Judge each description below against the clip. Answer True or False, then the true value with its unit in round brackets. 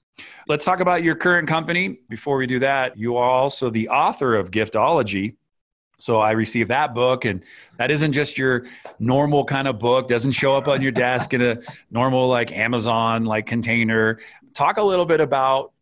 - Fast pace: False (185 wpm)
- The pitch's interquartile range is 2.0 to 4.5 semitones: True (3.1 semitones)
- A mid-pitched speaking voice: False (130 Hz)